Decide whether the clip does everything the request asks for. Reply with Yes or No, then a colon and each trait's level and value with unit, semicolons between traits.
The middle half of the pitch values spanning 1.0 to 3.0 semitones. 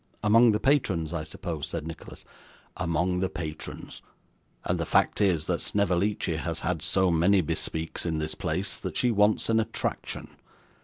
No: average, 4.2 semitones